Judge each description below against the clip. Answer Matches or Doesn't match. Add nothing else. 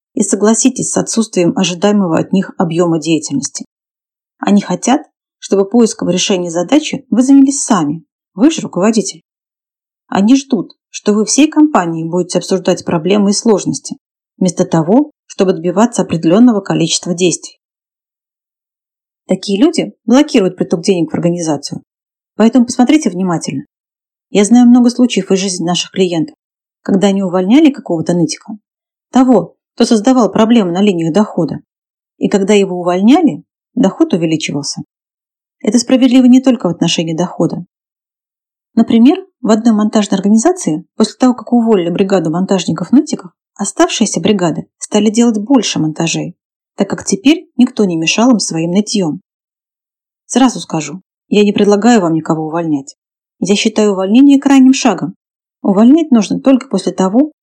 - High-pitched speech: Matches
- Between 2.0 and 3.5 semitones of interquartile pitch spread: Doesn't match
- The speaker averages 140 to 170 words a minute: Doesn't match